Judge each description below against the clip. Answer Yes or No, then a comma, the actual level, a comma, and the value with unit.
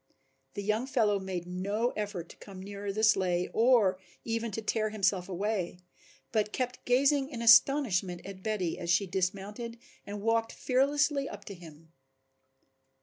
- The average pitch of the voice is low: No, high, 210 Hz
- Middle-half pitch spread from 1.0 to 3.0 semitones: No, average, 3.8 semitones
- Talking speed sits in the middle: Yes, average, 150 wpm